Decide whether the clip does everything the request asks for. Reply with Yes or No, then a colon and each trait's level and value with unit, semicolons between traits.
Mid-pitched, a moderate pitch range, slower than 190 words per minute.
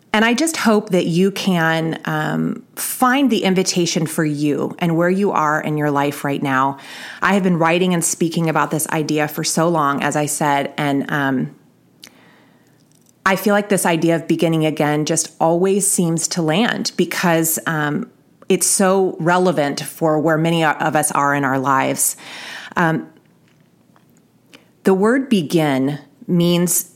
Yes: medium, 165 Hz; average, 3.7 semitones; average, 160 wpm